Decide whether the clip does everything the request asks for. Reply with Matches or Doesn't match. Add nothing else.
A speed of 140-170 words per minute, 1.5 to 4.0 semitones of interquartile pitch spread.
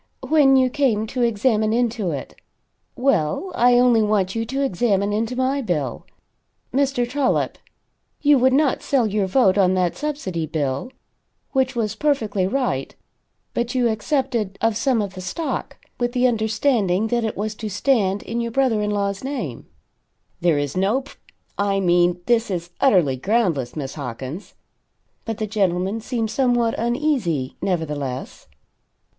Doesn't match